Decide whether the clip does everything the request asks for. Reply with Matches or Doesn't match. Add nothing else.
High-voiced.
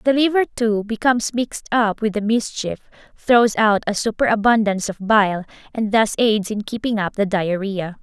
Matches